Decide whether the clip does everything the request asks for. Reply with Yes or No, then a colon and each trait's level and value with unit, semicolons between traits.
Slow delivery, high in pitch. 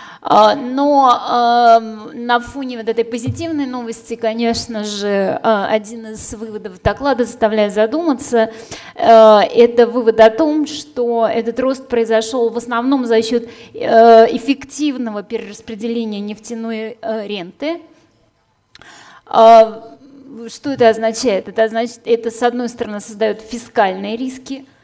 Yes: slow, 105 wpm; high, 230 Hz